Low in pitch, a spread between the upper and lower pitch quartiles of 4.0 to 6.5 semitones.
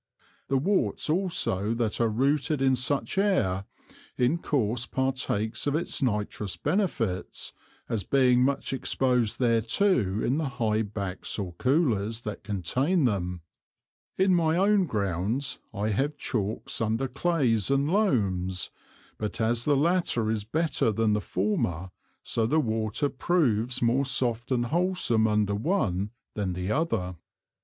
Yes: low, 120 Hz; wide, 5.4 semitones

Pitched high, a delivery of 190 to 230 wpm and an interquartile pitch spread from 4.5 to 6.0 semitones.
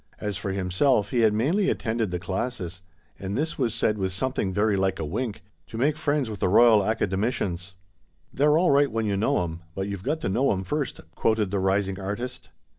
No: low, 105 Hz; fast, 205 wpm; average, 4.8 semitones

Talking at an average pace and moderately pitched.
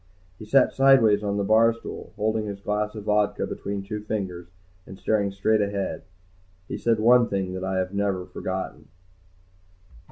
No: average, 165 wpm; low, 105 Hz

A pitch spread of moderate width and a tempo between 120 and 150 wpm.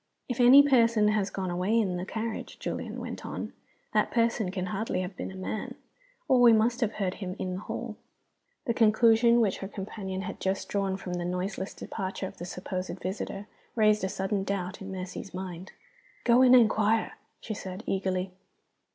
No: average, 3.2 semitones; average, 185 wpm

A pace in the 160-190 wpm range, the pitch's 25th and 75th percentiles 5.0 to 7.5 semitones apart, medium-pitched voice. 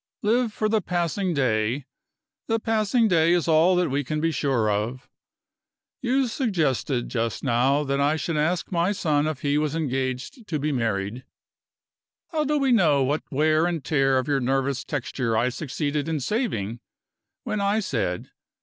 Yes: average, 170 wpm; wide, 5.6 semitones; medium, 150 Hz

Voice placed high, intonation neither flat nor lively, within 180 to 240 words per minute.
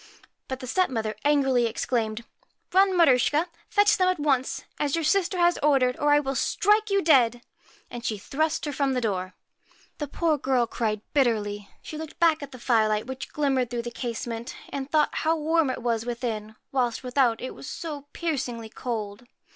Yes: very high, 260 Hz; average, 4.6 semitones; average, 190 wpm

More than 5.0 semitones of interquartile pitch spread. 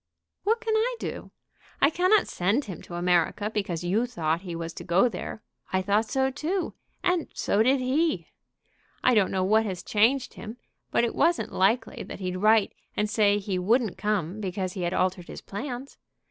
Yes: wide, 5.6 semitones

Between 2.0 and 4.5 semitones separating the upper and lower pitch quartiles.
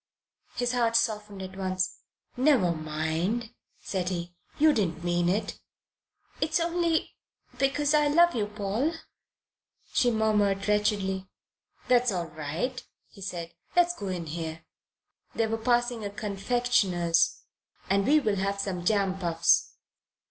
No: average, 5.1 semitones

